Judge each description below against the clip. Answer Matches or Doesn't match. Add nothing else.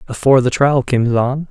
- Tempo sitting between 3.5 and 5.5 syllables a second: Matches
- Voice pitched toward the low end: Matches